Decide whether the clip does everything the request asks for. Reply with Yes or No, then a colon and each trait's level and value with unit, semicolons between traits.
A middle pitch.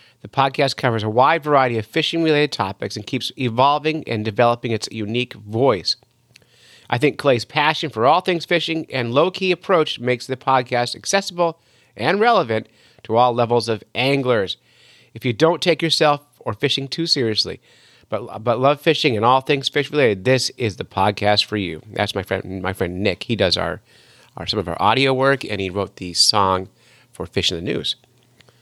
No: low, 125 Hz